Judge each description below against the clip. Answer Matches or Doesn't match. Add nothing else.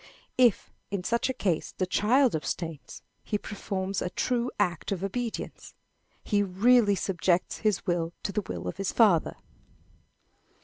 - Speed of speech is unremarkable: Matches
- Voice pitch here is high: Matches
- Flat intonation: Doesn't match